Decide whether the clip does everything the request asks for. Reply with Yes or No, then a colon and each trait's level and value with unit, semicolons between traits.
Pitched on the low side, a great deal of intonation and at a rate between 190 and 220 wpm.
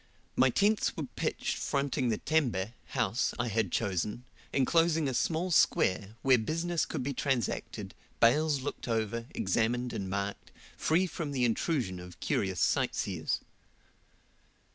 No: low, 125 Hz; wide, 6.2 semitones; slow, 135 wpm